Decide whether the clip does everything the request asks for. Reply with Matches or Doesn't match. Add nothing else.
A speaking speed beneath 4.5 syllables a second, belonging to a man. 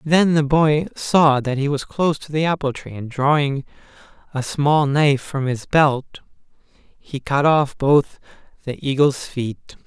Matches